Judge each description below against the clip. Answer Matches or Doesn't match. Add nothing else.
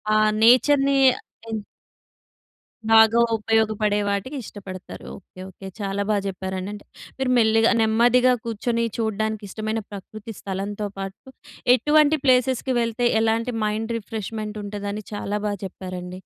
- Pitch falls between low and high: Doesn't match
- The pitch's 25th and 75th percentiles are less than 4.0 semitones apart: Matches